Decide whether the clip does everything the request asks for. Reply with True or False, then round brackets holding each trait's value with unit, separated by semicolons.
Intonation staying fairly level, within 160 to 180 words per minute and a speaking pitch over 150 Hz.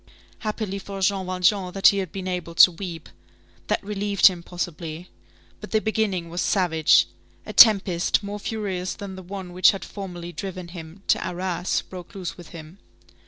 True (2.2 semitones; 170 wpm; 185 Hz)